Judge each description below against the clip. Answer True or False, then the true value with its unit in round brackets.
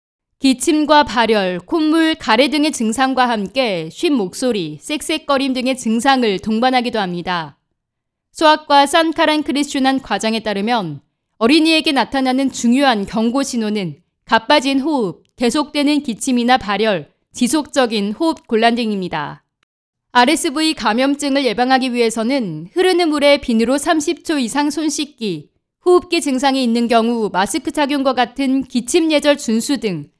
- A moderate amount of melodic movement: True (4.9 semitones)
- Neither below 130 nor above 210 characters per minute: False (300 characters per minute)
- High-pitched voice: True (260 Hz)